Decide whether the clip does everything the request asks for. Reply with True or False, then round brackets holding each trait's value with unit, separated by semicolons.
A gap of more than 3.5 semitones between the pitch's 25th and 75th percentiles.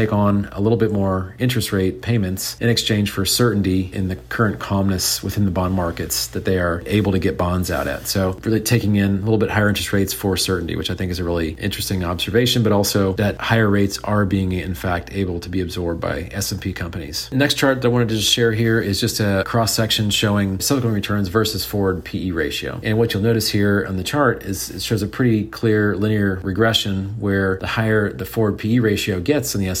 False (2.9 semitones)